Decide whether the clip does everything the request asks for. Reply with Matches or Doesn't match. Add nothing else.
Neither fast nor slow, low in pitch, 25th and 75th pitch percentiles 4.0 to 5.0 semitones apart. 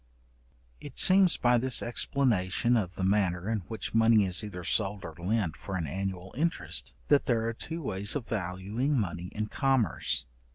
Matches